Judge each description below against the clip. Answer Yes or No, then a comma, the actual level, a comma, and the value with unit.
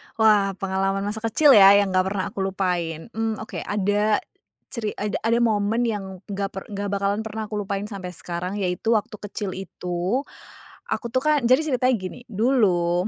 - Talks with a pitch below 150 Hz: No, high, 205 Hz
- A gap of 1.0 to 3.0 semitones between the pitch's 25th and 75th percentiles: Yes, narrow, 2.6 semitones